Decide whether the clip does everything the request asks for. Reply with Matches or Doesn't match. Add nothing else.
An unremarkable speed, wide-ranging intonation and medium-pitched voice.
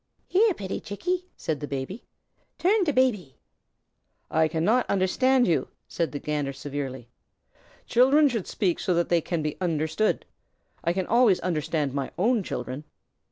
Matches